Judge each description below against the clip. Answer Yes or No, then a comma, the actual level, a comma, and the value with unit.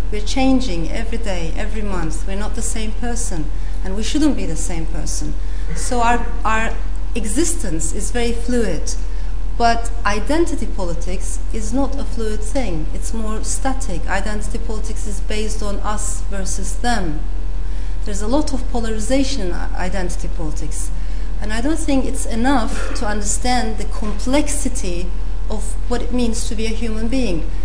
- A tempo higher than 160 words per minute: No, average, 155 wpm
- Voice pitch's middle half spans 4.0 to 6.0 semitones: No, average, 3.5 semitones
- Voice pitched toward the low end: No, high, 230 Hz